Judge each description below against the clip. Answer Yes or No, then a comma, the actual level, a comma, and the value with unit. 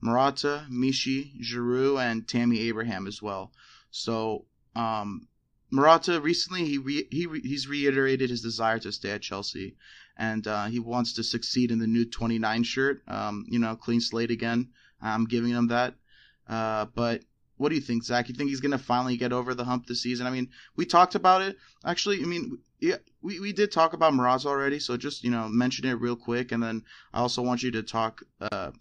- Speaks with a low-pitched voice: Yes, low, 120 Hz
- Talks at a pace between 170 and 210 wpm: Yes, fast, 205 wpm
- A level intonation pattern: No, average, 3.2 semitones